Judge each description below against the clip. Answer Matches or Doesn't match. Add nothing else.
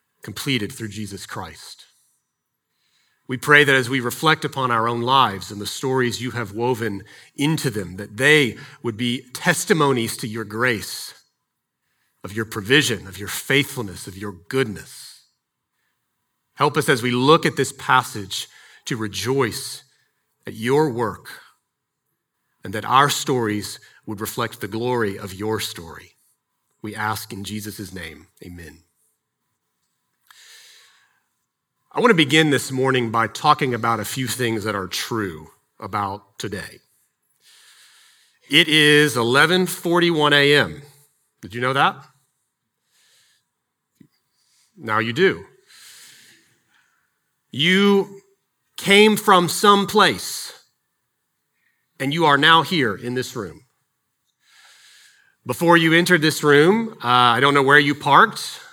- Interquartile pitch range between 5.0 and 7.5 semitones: Matches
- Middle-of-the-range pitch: Doesn't match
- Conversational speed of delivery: Doesn't match